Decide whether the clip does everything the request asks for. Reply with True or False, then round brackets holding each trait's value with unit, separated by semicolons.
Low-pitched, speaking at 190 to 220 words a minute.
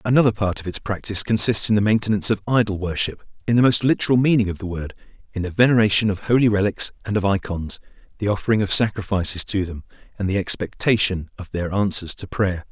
True (100 Hz; 205 wpm)